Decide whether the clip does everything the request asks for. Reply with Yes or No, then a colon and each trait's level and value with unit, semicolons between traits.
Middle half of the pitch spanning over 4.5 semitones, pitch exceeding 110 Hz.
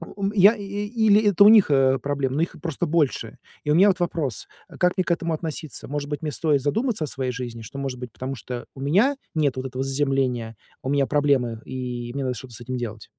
Yes: average, 5.0 semitones; medium, 140 Hz